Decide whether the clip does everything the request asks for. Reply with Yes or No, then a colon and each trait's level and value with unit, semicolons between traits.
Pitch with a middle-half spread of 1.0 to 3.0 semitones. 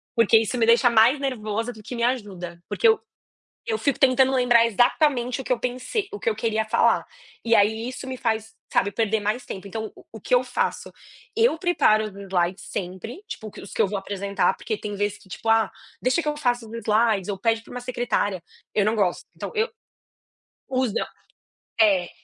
No: average, 3.5 semitones